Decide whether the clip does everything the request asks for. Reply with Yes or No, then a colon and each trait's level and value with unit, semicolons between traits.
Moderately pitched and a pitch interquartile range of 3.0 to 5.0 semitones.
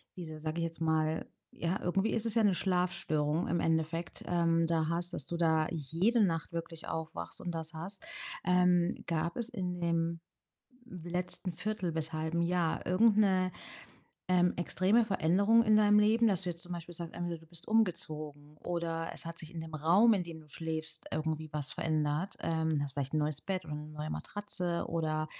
No: medium, 170 Hz; narrow, 2.4 semitones